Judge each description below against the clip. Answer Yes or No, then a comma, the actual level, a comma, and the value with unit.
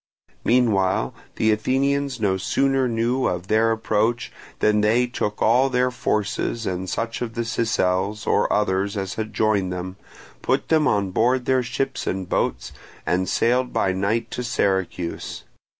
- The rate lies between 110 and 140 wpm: No, average, 150 wpm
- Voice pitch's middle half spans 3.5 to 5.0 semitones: Yes, average, 4.1 semitones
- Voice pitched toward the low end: Yes, low, 110 Hz